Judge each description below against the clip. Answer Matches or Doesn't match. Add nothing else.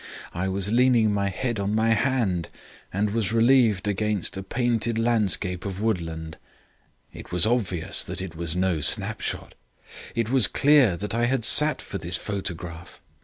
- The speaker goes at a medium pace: Matches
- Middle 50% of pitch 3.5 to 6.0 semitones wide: Matches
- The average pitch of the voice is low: Matches